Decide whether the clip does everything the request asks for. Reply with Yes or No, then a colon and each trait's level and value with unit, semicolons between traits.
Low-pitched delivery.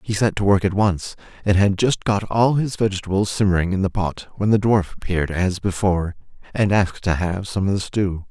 Yes: low, 100 Hz